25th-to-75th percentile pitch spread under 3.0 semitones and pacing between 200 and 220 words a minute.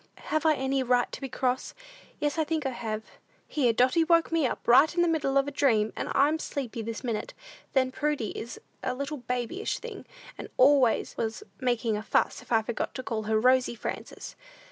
No: average, 3.9 semitones; fast, 205 wpm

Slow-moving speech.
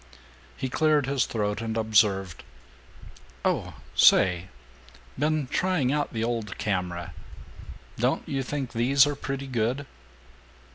Yes: slow, 115 wpm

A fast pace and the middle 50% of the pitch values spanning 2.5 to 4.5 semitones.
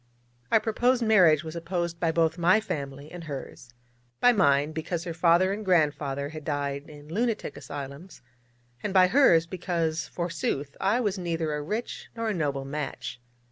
No: average, 165 wpm; average, 4.2 semitones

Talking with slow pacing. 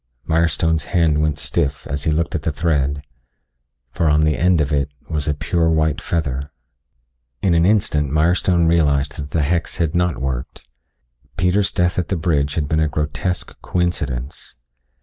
No: average, 170 wpm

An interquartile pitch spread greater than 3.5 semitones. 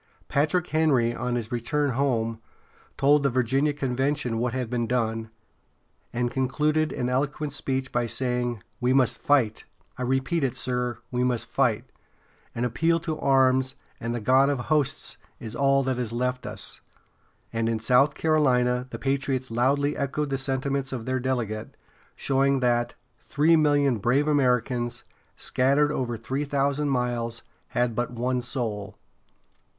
No: narrow, 2.5 semitones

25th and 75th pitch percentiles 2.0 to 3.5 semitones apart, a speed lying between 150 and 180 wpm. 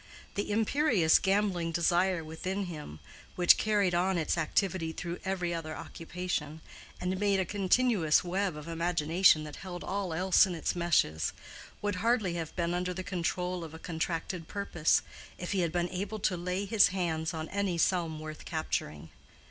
Yes: average, 2.8 semitones; average, 165 wpm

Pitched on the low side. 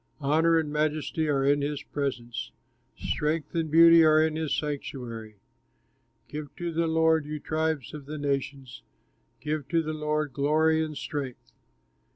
No: medium, 150 Hz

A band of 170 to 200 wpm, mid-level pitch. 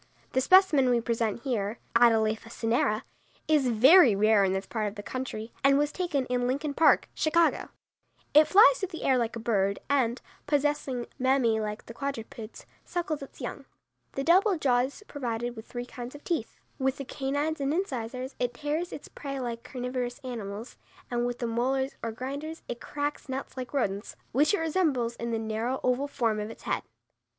No: average, 185 wpm; very high, 255 Hz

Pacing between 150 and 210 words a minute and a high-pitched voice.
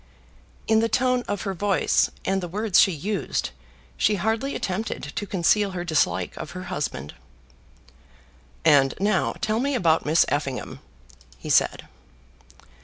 No: average, 140 wpm; high, 195 Hz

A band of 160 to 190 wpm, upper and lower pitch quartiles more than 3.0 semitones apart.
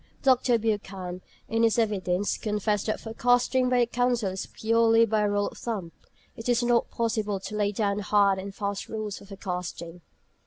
No: average, 170 wpm; narrow, 2.6 semitones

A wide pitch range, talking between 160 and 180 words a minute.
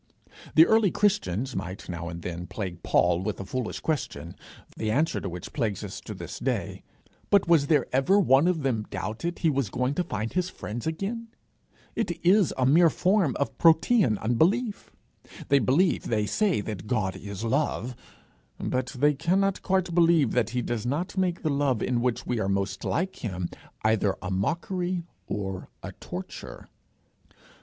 Yes: wide, 8.6 semitones; average, 170 wpm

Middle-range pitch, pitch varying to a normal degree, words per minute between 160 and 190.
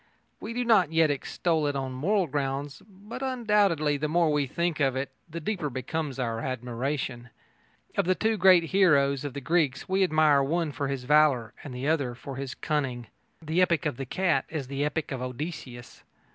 Yes: medium, 150 Hz; average, 4.2 semitones; average, 185 wpm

